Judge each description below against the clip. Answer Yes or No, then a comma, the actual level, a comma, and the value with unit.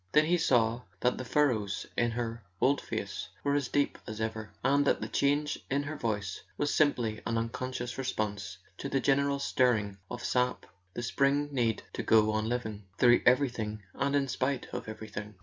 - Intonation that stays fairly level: No, average, 4.2 semitones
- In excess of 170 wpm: Yes, average, 185 wpm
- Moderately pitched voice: No, low, 125 Hz